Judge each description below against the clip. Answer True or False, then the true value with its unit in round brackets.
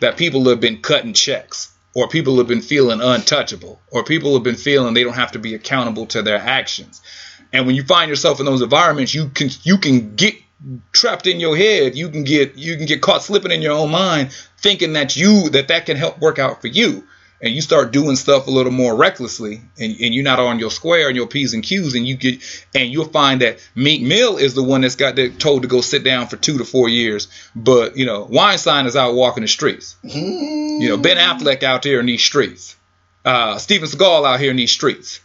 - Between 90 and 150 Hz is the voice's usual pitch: True (135 Hz)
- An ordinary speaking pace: False (235 wpm)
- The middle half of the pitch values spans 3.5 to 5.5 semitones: True (4.1 semitones)